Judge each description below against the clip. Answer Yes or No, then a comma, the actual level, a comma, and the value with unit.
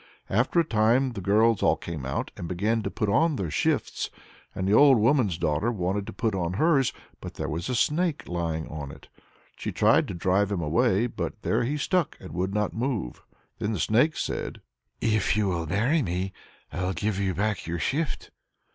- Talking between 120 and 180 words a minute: No, average, 195 wpm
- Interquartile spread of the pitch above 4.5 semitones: Yes, average, 5.2 semitones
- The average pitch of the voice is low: Yes, low, 105 Hz